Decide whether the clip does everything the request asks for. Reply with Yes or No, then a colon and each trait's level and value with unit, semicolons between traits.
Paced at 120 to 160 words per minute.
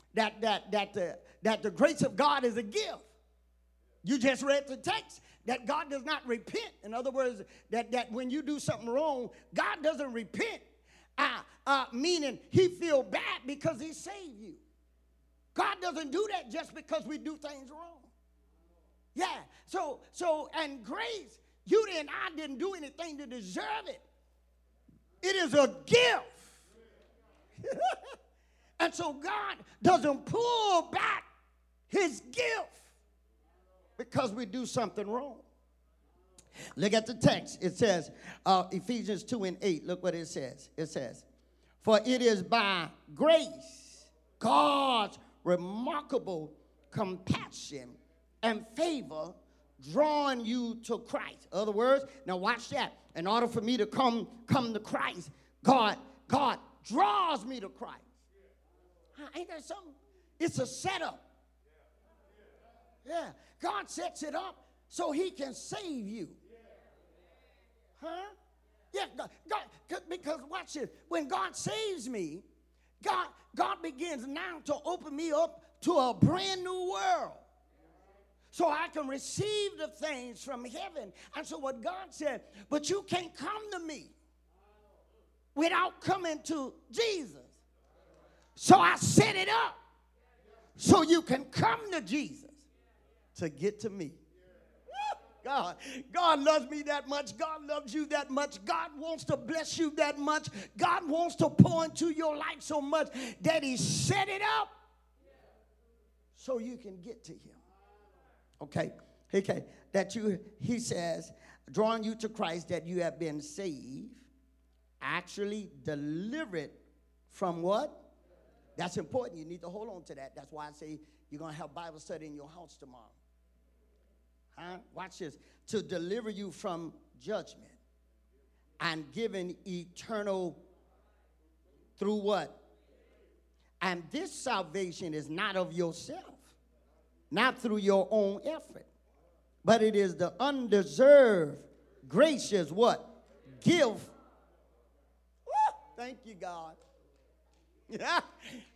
Yes: slow, 135 wpm